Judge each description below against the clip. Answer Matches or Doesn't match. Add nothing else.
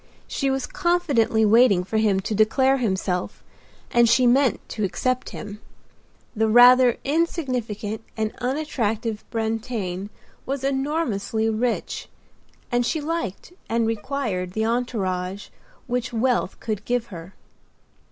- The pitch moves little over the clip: Doesn't match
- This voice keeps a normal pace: Doesn't match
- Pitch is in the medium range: Doesn't match